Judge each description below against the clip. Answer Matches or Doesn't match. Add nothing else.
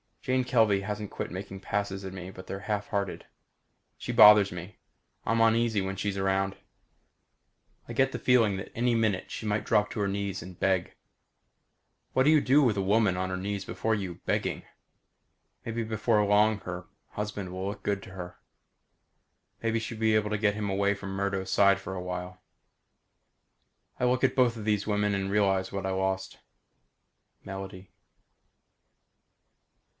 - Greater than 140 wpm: Matches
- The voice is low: Matches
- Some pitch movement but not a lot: Doesn't match